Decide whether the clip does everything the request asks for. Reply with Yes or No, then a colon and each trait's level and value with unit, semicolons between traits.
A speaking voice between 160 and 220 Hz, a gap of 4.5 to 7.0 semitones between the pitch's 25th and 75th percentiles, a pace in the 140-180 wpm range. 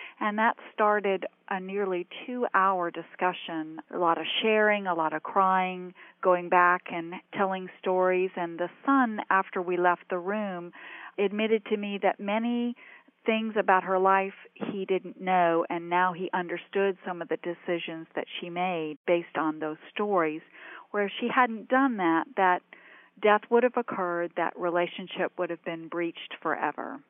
No: medium, 185 Hz; average, 3.1 semitones; average, 165 wpm